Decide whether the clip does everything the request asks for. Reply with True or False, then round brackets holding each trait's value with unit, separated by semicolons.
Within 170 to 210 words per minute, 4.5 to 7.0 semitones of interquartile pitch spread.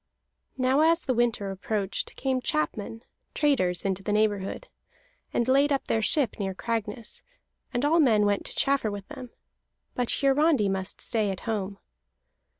False (150 wpm; 5.1 semitones)